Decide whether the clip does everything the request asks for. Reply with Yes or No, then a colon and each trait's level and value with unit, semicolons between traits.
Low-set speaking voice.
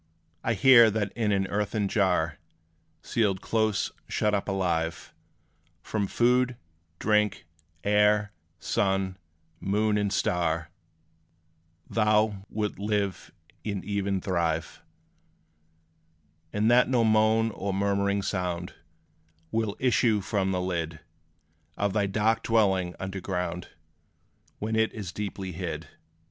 Yes: low, 100 Hz